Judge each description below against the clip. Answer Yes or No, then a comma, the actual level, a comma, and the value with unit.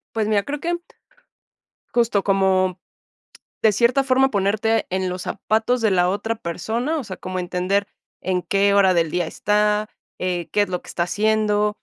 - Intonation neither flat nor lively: Yes, average, 3.1 semitones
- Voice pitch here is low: No, high, 205 Hz